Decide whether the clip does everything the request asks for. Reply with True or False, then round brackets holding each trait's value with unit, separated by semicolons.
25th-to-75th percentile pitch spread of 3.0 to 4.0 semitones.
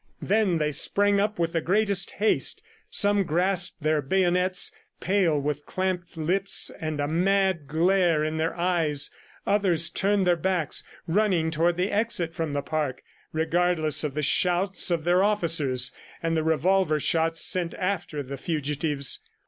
True (3.4 semitones)